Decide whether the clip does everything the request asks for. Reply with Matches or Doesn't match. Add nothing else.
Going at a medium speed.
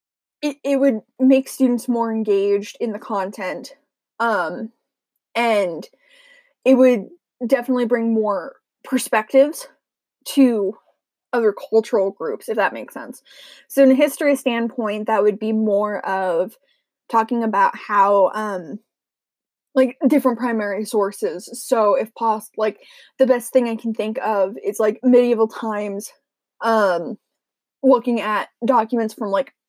Doesn't match